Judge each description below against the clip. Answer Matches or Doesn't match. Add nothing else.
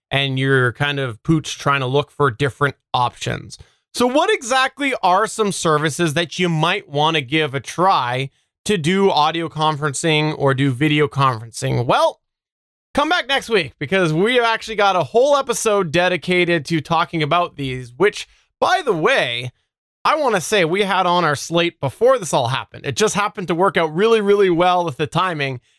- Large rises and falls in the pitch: Matches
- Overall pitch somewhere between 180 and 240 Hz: Doesn't match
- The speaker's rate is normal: Matches